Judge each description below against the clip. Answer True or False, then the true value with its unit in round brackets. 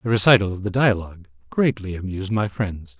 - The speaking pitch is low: True (100 Hz)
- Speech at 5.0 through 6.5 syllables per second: True (6.0 syllables/s)